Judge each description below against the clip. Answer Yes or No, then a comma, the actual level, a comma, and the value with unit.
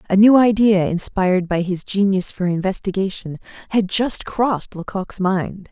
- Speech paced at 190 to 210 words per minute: No, average, 145 wpm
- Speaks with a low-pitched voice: No, high, 195 Hz